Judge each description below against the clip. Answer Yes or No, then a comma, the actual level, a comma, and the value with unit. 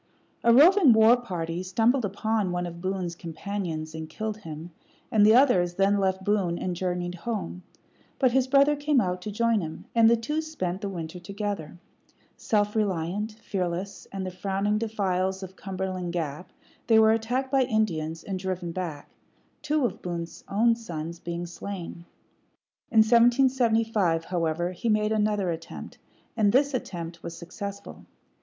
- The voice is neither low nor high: No, high, 195 Hz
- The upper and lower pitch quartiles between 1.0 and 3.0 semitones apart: No, average, 4.3 semitones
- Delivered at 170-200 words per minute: No, average, 155 wpm